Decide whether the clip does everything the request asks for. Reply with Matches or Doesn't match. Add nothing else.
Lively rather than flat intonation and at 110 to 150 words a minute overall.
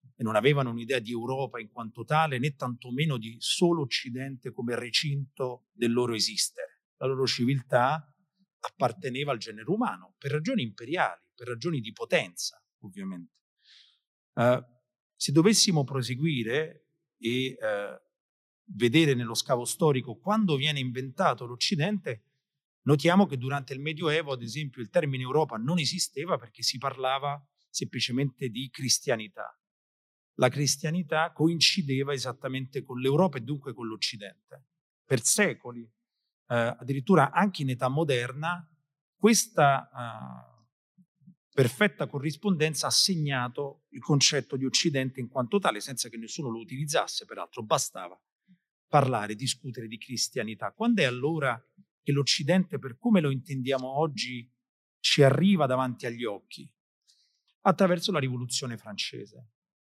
Doesn't match